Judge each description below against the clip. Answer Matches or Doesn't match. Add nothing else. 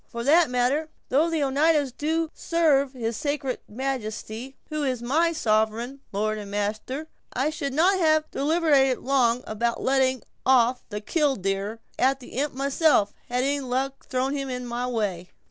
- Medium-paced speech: Matches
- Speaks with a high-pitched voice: Matches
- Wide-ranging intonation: Doesn't match